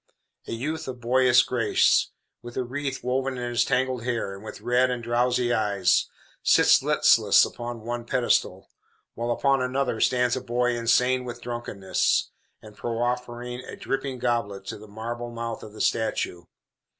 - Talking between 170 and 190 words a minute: No, average, 160 wpm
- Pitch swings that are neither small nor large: No, narrow, 1.5 semitones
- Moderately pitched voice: No, low, 120 Hz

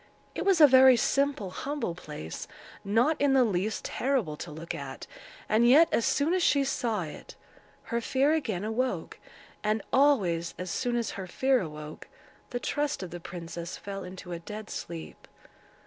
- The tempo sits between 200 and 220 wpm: No, average, 170 wpm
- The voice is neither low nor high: No, high, 220 Hz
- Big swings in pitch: Yes, wide, 7.4 semitones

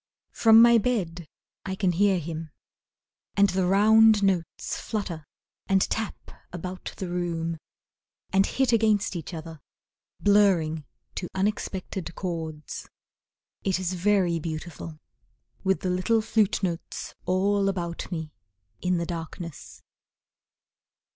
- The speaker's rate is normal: No, slow, 115 wpm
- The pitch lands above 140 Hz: Yes, medium, 185 Hz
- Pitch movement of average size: Yes, average, 3.2 semitones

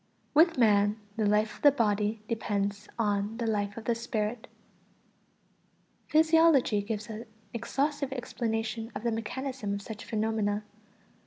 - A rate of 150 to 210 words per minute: No, slow, 135 wpm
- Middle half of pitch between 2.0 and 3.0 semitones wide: Yes, narrow, 2.6 semitones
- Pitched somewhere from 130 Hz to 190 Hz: No, high, 225 Hz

